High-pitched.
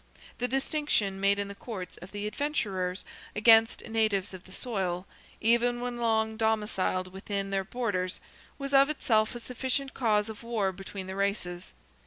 Yes: high, 215 Hz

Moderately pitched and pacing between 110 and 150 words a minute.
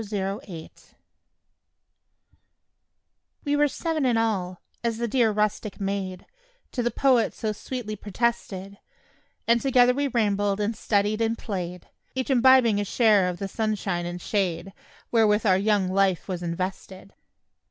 No: high, 210 Hz; average, 140 wpm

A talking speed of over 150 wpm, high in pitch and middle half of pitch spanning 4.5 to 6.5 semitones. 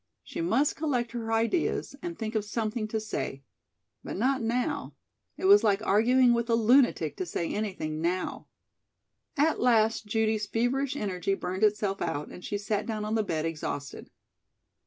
No: average, 165 wpm; high, 220 Hz; average, 3.2 semitones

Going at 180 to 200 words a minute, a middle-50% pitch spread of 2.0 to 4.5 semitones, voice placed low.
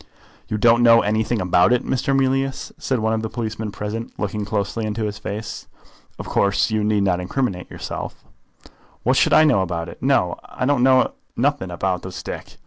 Yes: average, 185 wpm; average, 3.3 semitones; low, 110 Hz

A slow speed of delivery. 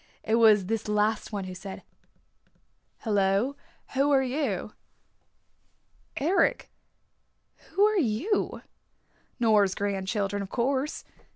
Yes: slow, 100 wpm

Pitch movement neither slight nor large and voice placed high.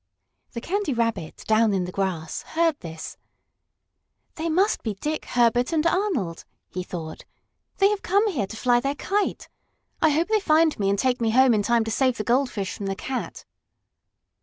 No: wide, 7.9 semitones; high, 245 Hz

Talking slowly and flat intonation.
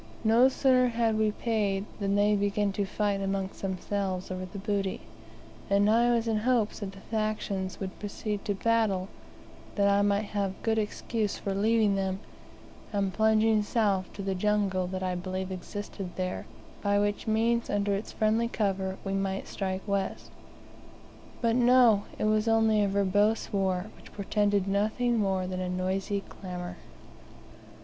No: average, 160 wpm; narrow, 2.1 semitones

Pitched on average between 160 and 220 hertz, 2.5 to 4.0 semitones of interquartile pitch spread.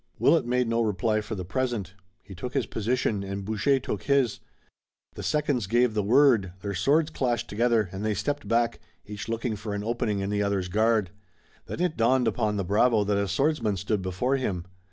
No: low, 110 Hz; average, 3.7 semitones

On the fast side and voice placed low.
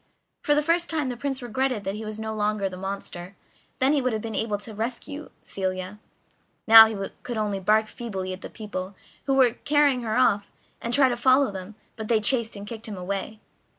No: fast, 215 wpm; high, 220 Hz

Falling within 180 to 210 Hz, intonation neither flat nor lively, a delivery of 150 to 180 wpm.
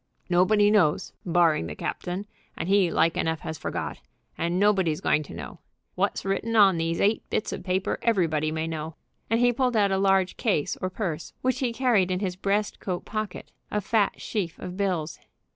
No: medium, 185 Hz; average, 4.0 semitones; average, 195 wpm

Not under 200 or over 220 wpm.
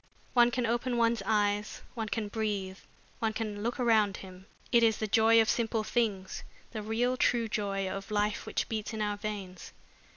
No: average, 185 wpm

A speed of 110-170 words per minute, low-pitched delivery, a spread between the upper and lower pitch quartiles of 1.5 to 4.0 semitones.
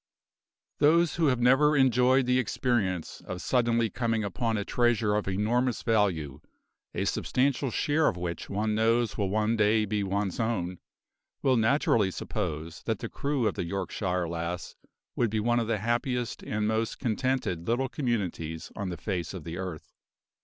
No: average, 165 wpm; low, 110 Hz; average, 4.6 semitones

